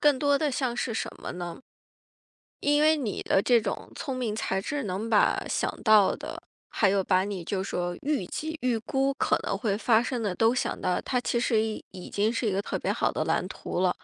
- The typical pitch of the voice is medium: No, high, 225 Hz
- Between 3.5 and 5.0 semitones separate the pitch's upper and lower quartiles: Yes, average, 4.7 semitones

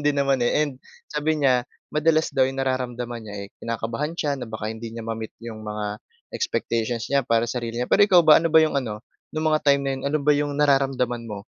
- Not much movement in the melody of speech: No, average, 4.3 semitones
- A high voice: No, low, 130 Hz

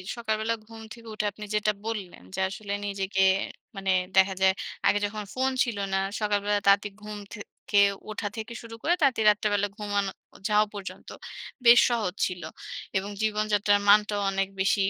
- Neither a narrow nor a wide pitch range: No, narrow, 1.5 semitones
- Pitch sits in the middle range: No, high, 210 Hz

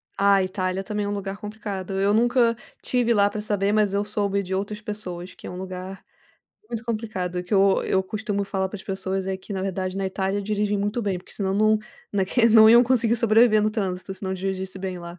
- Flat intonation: Yes, narrow, 2.1 semitones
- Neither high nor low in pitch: No, high, 200 Hz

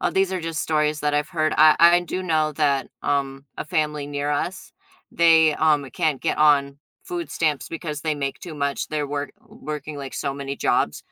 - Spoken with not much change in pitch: Yes, narrow, 2.1 semitones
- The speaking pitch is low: No, medium, 150 Hz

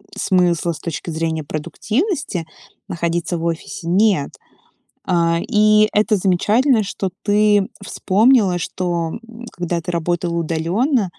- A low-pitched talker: No, medium, 180 Hz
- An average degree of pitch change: Yes, average, 3.9 semitones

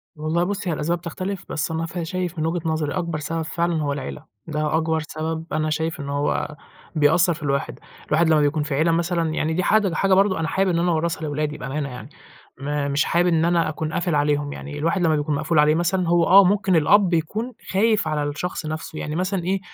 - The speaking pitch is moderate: Yes, medium, 160 Hz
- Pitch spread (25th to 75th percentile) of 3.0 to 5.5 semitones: No, narrow, 2.5 semitones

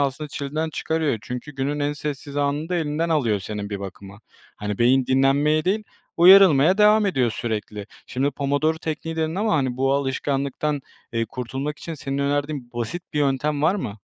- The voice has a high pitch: No, medium, 140 Hz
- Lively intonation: No, average, 3.4 semitones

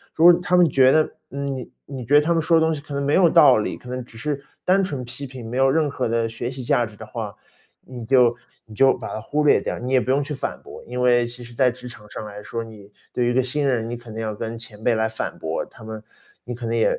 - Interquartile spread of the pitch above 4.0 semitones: No, average, 3.5 semitones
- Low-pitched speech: Yes, low, 125 Hz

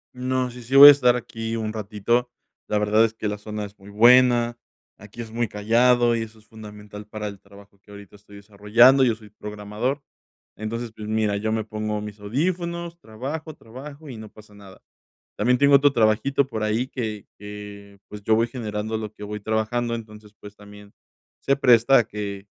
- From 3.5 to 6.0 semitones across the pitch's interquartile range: No, average, 2.8 semitones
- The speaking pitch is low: Yes, low, 110 Hz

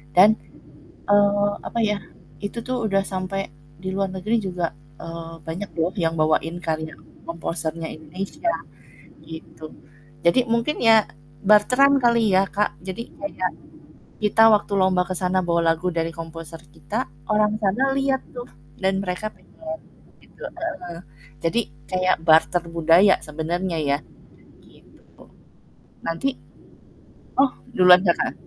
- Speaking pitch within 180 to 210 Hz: Yes, medium, 185 Hz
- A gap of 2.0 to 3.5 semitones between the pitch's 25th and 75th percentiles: No, average, 4.2 semitones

